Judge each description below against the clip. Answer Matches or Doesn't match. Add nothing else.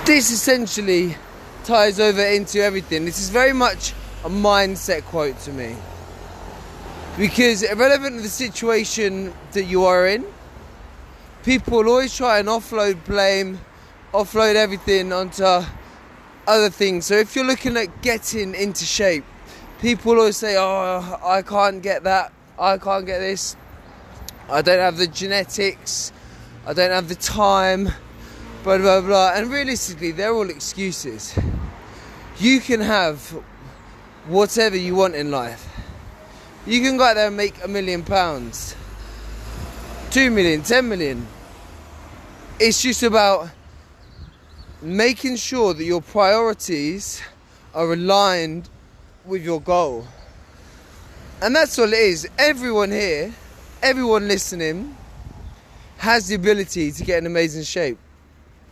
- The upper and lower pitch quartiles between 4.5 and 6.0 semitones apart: Matches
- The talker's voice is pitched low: Doesn't match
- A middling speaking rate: Doesn't match